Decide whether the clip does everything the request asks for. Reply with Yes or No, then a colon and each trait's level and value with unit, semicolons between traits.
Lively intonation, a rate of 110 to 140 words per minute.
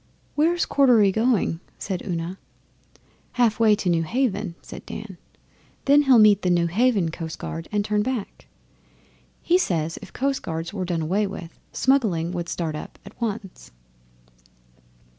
Yes: wide, 5.7 semitones; slow, 135 wpm